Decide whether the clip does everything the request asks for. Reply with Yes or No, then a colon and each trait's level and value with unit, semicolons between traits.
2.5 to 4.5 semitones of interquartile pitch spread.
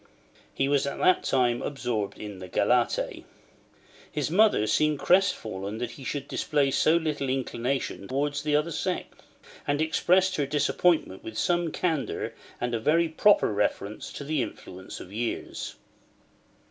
No: average, 5.2 semitones